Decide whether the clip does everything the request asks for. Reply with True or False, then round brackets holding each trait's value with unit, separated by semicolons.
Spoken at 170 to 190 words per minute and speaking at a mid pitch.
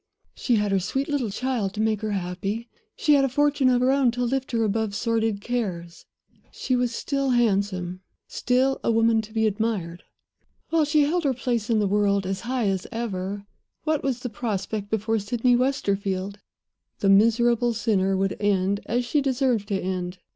False (185 wpm; 225 Hz)